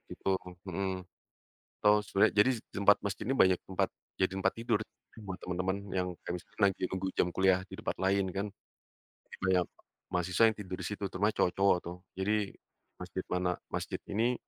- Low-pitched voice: Yes, very low, 95 Hz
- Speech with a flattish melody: Yes, narrow, 1.7 semitones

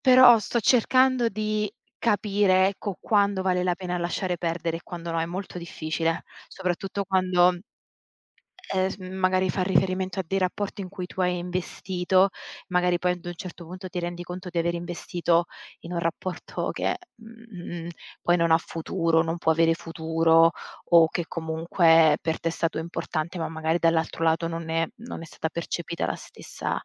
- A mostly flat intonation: Yes, narrow, 2.3 semitones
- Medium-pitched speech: Yes, medium, 175 Hz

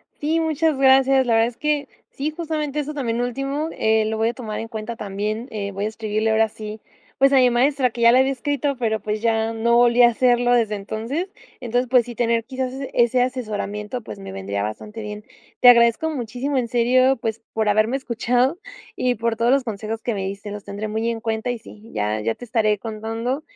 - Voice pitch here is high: Yes, high, 235 Hz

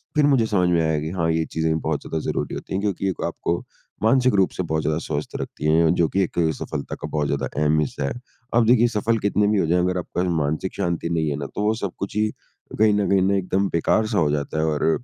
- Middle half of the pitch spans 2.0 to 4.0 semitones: No, average, 4.5 semitones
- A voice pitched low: Yes, very low, 90 Hz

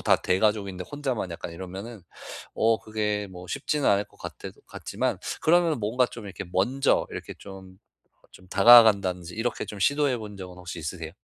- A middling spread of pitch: Yes, average, 4.6 semitones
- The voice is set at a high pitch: No, low, 105 Hz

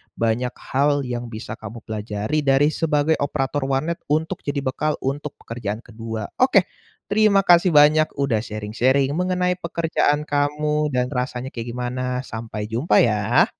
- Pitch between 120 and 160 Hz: Yes, low, 135 Hz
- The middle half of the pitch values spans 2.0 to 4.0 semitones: No, average, 4.5 semitones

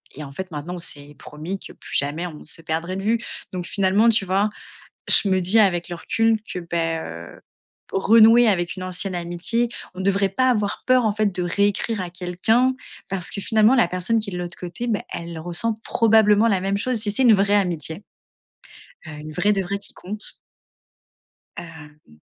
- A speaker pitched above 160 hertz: Yes, high, 190 Hz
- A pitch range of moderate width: Yes, average, 3.8 semitones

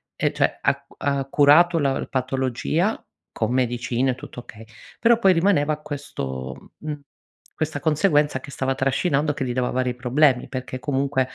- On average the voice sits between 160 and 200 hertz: No, low, 135 Hz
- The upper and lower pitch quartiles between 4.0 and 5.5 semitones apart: No, average, 2.9 semitones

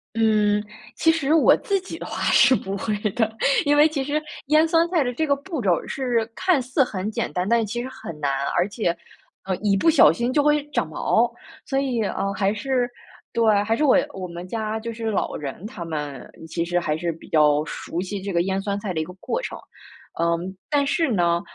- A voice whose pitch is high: Yes, high, 220 Hz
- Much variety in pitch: Yes, wide, 7.1 semitones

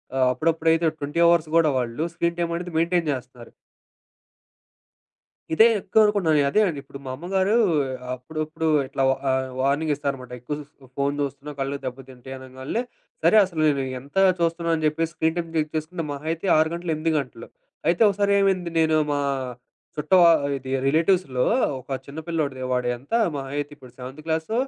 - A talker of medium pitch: Yes, medium, 155 Hz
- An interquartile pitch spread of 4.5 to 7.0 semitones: No, average, 3.8 semitones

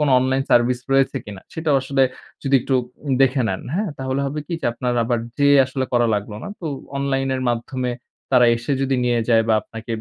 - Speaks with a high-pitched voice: No, low, 130 Hz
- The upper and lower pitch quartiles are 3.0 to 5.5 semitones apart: No, narrow, 2.4 semitones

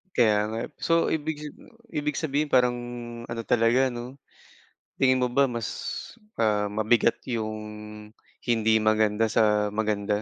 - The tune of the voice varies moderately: Yes, average, 3.3 semitones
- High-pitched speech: No, low, 115 Hz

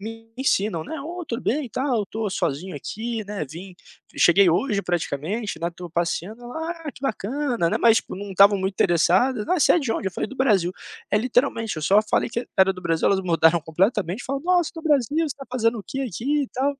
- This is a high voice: Yes, high, 215 Hz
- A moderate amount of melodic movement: No, wide, 6.4 semitones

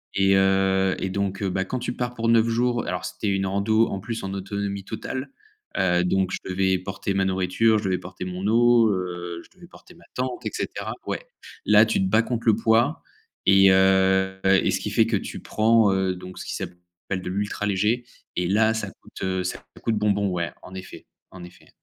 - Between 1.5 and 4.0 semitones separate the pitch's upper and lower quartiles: Yes, average, 2.9 semitones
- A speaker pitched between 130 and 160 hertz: No, very low, 95 Hz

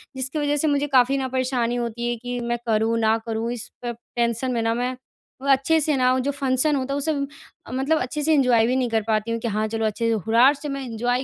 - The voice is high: Yes, very high, 250 Hz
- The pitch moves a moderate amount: Yes, average, 3.0 semitones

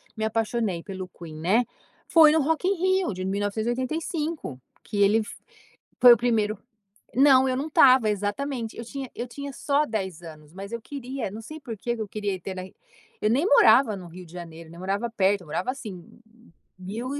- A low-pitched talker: No, high, 220 Hz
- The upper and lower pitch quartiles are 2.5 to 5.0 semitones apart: No, wide, 5.6 semitones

